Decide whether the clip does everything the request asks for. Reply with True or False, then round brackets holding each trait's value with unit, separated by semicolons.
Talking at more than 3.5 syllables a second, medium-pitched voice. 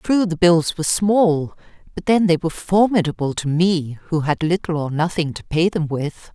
True (5.1 syllables/s; 170 Hz)